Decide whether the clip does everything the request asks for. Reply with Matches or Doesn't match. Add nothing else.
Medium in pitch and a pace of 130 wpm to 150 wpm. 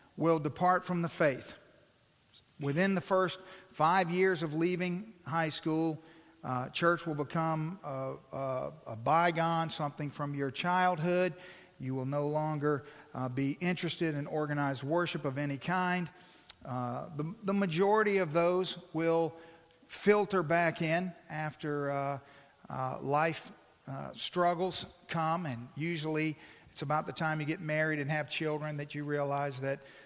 Matches